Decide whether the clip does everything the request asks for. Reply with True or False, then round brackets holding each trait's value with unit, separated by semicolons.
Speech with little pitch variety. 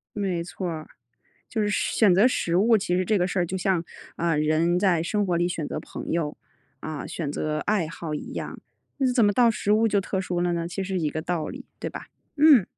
False (3.6 semitones)